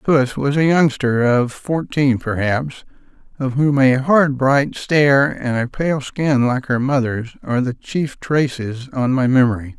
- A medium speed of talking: Yes, average, 165 wpm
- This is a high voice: No, low, 135 Hz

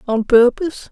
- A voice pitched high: Yes, very high, 255 Hz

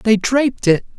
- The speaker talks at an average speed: Yes, average, 185 wpm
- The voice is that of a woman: No, male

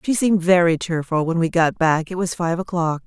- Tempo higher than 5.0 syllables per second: Yes, 5.4 syllables/s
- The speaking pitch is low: No, medium, 175 Hz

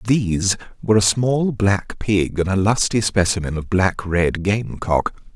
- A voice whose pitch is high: No, low, 100 Hz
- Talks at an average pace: Yes, average, 155 wpm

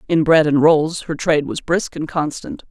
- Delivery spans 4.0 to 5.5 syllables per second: Yes, 4.9 syllables/s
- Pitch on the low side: No, medium, 155 Hz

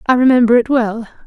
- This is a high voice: Yes, high, 240 Hz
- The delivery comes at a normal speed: Yes, average, 190 wpm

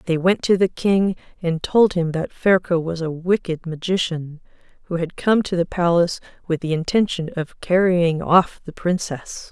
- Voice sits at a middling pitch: Yes, medium, 175 Hz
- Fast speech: No, average, 175 wpm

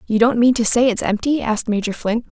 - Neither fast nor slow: No, fast, 255 wpm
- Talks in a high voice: Yes, high, 230 Hz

